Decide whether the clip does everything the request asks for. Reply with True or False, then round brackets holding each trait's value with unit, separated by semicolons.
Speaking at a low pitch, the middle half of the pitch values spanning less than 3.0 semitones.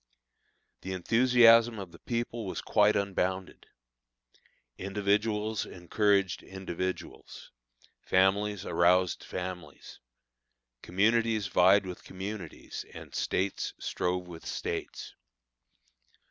True (95 Hz; 2.6 semitones)